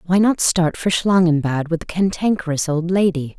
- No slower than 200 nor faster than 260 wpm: No, average, 175 wpm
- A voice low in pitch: No, medium, 175 Hz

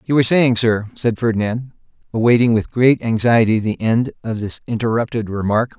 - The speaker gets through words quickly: No, average, 155 wpm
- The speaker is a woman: No, male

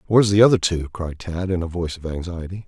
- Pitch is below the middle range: Yes, very low, 90 Hz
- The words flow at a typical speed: No, fast, 245 wpm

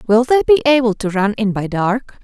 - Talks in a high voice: Yes, high, 230 Hz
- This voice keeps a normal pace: No, fast, 240 wpm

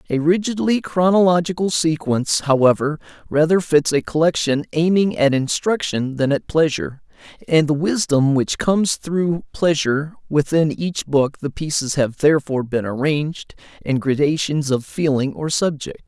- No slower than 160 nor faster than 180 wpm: No, slow, 135 wpm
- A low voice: No, medium, 155 Hz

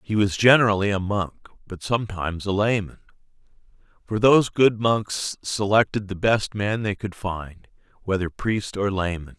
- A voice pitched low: Yes, low, 100 Hz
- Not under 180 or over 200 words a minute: No, average, 155 wpm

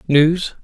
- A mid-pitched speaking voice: Yes, medium, 160 Hz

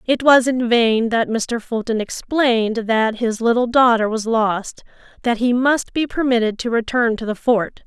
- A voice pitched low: No, high, 235 Hz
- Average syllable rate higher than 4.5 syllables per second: No, 4.4 syllables/s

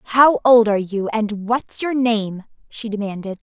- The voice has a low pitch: No, high, 220 Hz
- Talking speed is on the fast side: No, average, 170 wpm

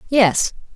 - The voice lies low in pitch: No, high, 230 Hz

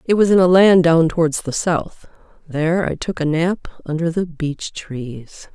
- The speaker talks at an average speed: Yes, average, 185 wpm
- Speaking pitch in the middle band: Yes, medium, 165 Hz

